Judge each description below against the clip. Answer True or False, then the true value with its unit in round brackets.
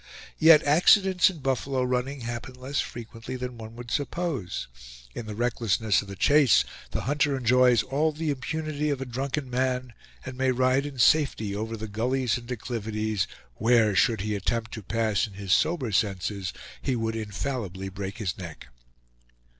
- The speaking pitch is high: False (120 Hz)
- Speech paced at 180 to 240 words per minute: False (165 wpm)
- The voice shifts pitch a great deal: False (3.8 semitones)